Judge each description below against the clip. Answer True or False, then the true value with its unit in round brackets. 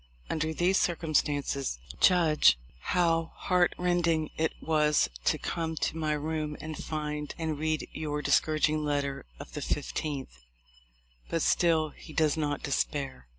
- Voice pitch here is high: False (155 Hz)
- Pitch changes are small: True (1.6 semitones)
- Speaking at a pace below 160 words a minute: True (135 wpm)